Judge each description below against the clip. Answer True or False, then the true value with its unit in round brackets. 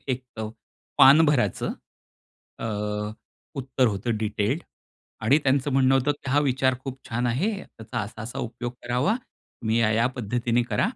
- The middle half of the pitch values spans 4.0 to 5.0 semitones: False (2.9 semitones)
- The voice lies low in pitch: True (125 Hz)